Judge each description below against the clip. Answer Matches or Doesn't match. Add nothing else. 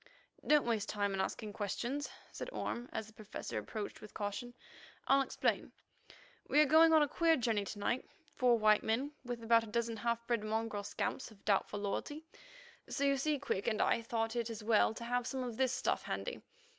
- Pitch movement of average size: Matches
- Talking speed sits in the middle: Matches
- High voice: Matches